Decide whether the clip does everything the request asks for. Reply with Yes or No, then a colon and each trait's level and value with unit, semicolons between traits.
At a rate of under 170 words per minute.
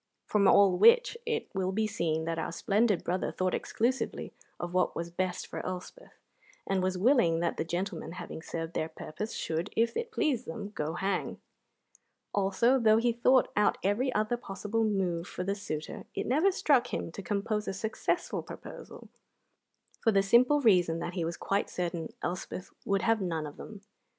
No: average, 180 wpm